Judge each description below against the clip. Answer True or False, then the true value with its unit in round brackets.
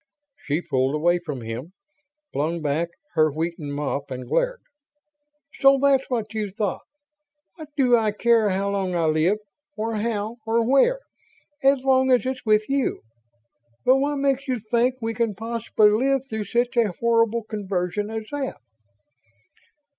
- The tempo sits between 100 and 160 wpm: True (155 wpm)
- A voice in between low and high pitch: False (220 Hz)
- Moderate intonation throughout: False (6.4 semitones)